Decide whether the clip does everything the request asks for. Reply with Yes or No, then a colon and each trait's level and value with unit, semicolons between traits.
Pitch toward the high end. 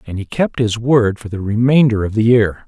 No: low, 115 Hz